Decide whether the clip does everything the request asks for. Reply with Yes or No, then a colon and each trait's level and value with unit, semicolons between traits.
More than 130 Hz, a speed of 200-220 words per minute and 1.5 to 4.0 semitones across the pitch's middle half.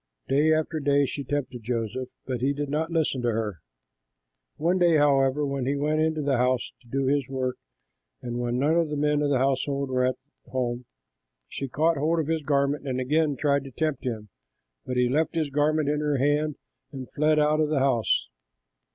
Yes: medium, 140 Hz; fast, 205 wpm; average, 2.8 semitones